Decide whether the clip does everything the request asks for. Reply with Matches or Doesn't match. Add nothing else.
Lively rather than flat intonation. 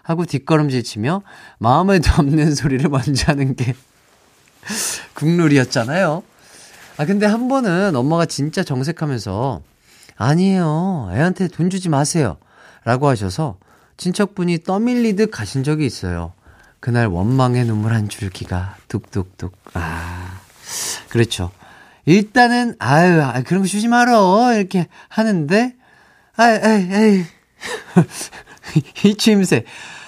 Matches